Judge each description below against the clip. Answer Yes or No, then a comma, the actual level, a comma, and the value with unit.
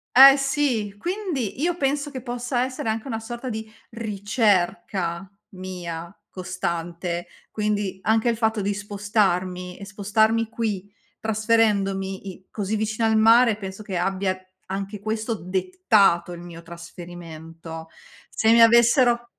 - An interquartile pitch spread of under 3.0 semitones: No, average, 3.7 semitones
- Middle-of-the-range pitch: No, high, 210 Hz